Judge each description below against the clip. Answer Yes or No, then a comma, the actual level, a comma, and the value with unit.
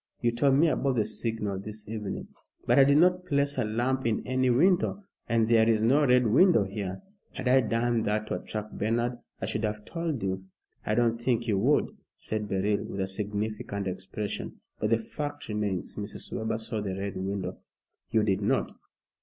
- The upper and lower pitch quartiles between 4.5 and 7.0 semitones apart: No, average, 3.4 semitones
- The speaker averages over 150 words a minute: Yes, average, 190 wpm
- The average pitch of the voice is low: Yes, low, 110 Hz